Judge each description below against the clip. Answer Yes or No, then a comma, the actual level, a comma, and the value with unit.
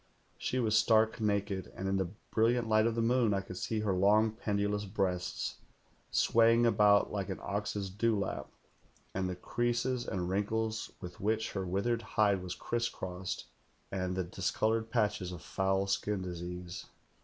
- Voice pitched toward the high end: No, low, 105 Hz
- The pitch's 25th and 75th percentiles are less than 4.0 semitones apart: Yes, average, 2.9 semitones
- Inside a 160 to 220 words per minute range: Yes, average, 165 wpm